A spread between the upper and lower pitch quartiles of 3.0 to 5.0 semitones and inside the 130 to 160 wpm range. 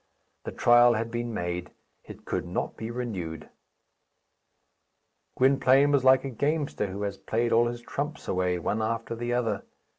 Yes: average, 3.5 semitones; average, 155 wpm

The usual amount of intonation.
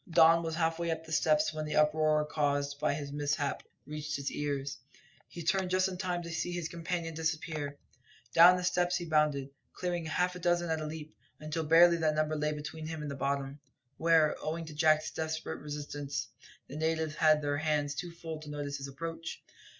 No: narrow, 2.0 semitones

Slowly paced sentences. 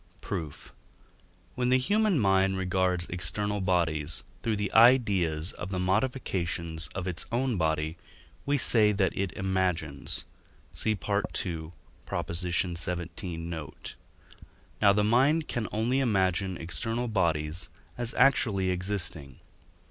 Yes: slow, 115 wpm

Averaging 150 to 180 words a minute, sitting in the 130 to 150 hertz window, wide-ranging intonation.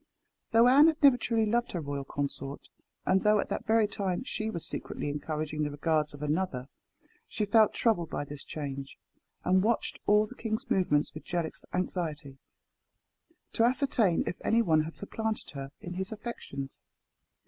No: average, 170 wpm; medium, 180 Hz; wide, 6.9 semitones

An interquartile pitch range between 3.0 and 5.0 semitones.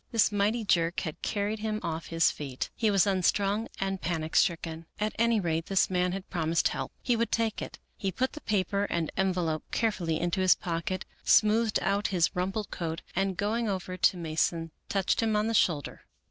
Yes: average, 3.9 semitones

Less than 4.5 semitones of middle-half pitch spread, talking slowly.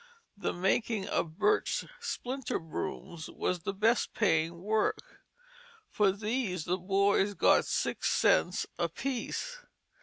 No: average, 4.8 semitones; slow, 115 wpm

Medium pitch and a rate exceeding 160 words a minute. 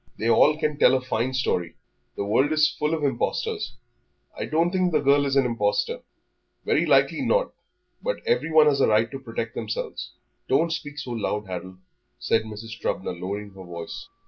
No: low, 130 Hz; average, 180 wpm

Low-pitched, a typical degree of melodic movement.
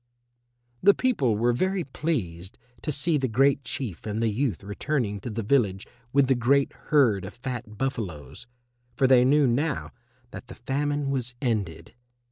Yes: low, 125 Hz; average, 4.6 semitones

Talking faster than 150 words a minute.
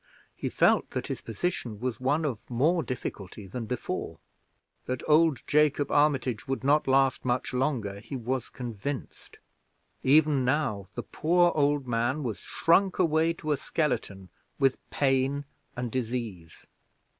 No: average, 140 wpm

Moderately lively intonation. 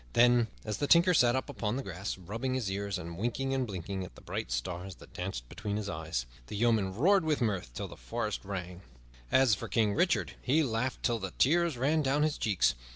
No: wide, 5.9 semitones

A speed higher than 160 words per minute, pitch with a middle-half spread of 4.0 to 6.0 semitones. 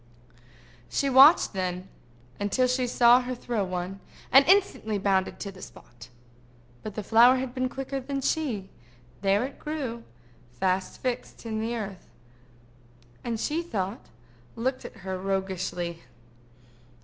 No: slow, 135 wpm; average, 5.1 semitones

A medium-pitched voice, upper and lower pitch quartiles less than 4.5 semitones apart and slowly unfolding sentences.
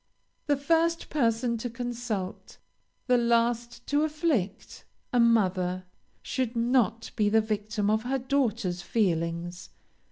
No: high, 230 Hz; average, 3.4 semitones; slow, 120 wpm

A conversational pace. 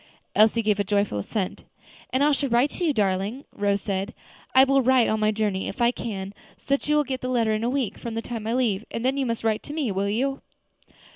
No: fast, 255 wpm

